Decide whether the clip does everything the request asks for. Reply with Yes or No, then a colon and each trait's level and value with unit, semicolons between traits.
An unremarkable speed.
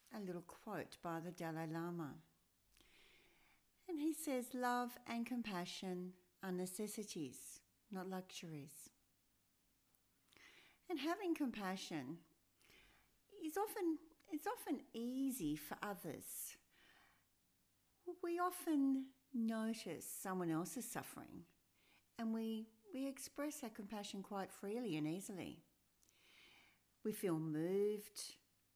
No: slow, 95 wpm